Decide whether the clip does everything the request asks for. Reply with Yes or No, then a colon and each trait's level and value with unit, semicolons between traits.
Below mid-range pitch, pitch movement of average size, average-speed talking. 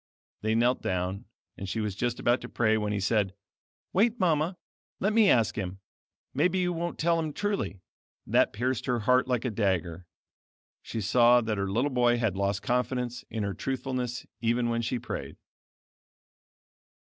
Yes: low, 120 Hz; average, 4.0 semitones; average, 170 wpm